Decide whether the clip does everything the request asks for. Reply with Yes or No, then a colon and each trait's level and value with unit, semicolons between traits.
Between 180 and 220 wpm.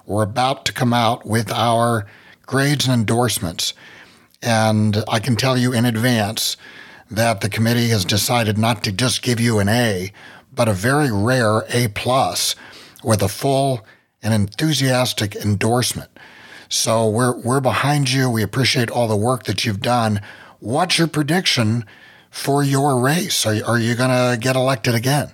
No: average, 160 wpm